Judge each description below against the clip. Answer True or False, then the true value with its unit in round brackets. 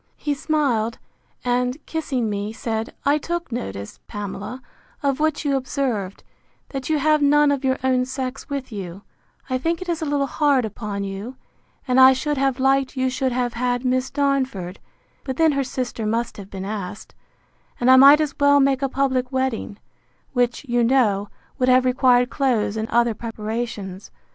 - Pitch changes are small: False (3.6 semitones)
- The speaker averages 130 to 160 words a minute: False (175 wpm)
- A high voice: True (255 Hz)